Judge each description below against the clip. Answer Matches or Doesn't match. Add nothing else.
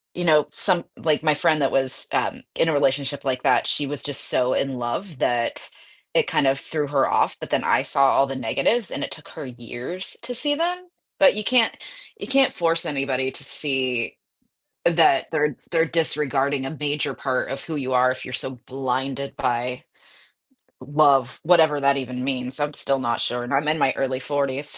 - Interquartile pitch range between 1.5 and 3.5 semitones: Matches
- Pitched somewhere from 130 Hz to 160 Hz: Matches